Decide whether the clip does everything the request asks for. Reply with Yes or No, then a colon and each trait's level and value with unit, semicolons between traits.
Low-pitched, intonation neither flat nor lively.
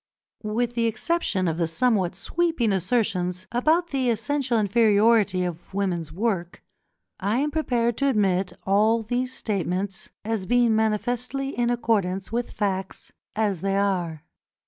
No: high, 215 Hz; average, 4.2 semitones